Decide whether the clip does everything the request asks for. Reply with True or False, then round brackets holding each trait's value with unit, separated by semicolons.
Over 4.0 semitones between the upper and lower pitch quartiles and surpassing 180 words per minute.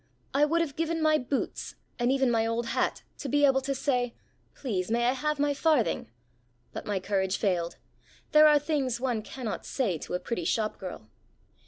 True (5.1 semitones; 190 wpm)